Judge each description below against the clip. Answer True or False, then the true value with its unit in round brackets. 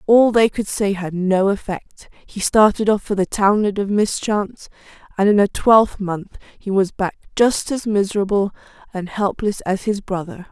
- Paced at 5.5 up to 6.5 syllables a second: False (4.6 syllables/s)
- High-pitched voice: True (200 Hz)